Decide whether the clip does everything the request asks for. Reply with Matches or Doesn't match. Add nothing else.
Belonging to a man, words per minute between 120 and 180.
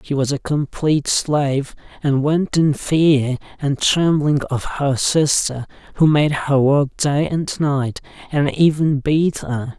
Matches